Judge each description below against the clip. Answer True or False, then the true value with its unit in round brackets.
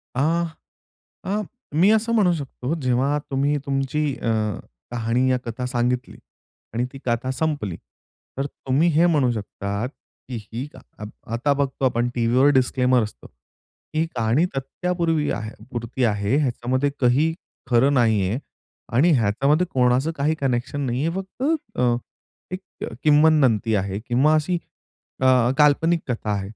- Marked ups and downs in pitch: False (4.1 semitones)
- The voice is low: True (130 Hz)